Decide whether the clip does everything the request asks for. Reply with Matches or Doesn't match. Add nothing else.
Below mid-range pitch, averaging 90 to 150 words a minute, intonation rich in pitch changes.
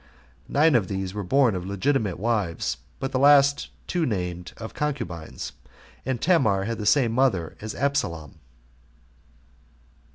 Matches